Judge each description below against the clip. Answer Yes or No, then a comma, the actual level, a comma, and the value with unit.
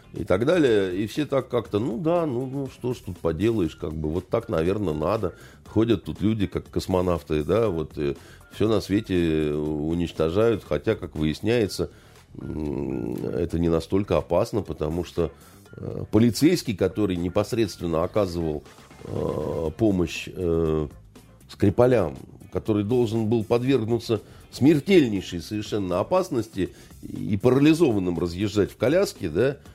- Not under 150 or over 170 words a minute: No, average, 120 wpm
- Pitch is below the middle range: Yes, very low, 95 Hz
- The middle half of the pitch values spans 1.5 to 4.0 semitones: No, wide, 5.5 semitones